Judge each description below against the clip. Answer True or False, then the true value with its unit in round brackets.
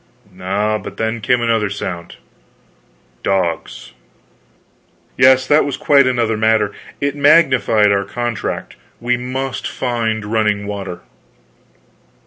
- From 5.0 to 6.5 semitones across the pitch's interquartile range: False (3.8 semitones)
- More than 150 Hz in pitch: False (110 Hz)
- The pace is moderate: False (110 wpm)